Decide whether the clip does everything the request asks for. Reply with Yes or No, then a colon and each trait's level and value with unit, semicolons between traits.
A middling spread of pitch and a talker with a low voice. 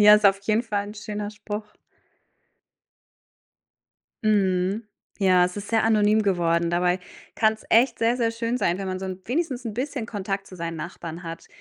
No: average, 3.2 semitones; high, 205 Hz